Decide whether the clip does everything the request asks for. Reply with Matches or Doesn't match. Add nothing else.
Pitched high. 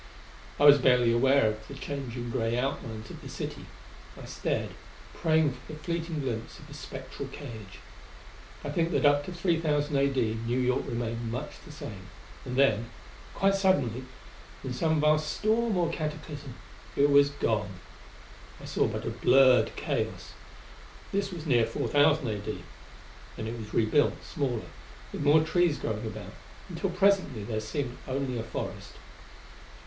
Doesn't match